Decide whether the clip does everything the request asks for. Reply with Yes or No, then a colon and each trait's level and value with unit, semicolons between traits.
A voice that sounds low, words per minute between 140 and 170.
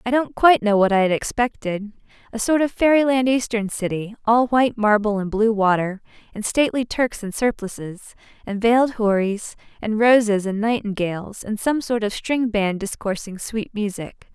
No: high, 220 Hz; average, 165 wpm